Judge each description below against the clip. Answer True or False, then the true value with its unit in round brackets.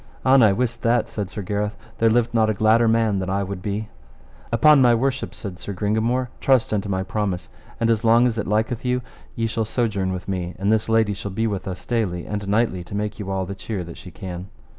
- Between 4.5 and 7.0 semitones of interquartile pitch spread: False (2.9 semitones)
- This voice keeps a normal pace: False (235 wpm)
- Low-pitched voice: True (105 Hz)